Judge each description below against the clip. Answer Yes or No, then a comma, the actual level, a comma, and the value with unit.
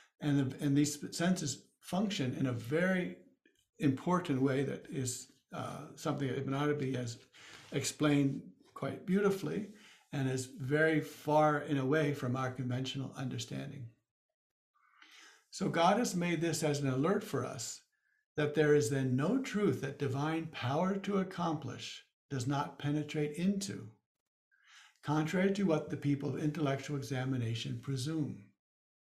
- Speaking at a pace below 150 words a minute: Yes, average, 140 wpm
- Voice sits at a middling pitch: Yes, medium, 145 Hz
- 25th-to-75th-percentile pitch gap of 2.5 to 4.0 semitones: Yes, average, 2.9 semitones